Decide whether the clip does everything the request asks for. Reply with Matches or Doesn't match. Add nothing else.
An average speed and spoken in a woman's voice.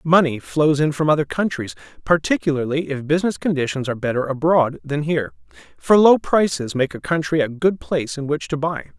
Doesn't match